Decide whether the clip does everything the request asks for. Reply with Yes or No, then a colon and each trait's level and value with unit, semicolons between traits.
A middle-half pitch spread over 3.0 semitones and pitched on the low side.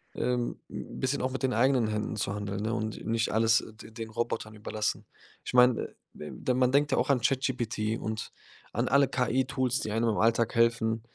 No: narrow, 2.6 semitones; low, 115 Hz